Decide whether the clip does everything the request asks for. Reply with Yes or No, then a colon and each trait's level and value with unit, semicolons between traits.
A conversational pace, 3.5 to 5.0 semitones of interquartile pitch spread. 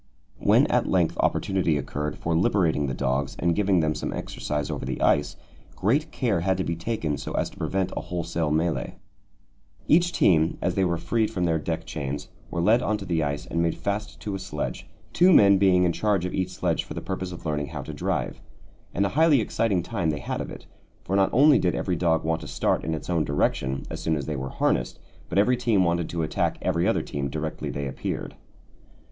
No: fast, 225 wpm; average, 4.1 semitones